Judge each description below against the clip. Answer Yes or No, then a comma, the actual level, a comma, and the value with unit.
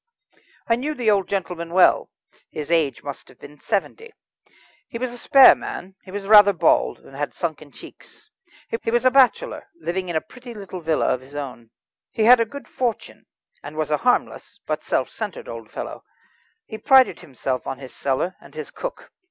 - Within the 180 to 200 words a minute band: Yes, average, 190 wpm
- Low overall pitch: No, high, 190 Hz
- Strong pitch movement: Yes, wide, 8.2 semitones